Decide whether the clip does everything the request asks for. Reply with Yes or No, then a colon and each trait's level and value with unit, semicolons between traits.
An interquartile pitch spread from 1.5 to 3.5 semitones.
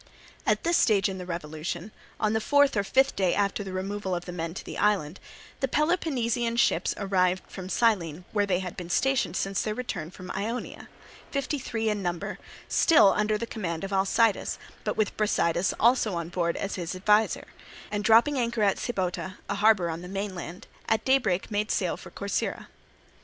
No: average, 3.9 semitones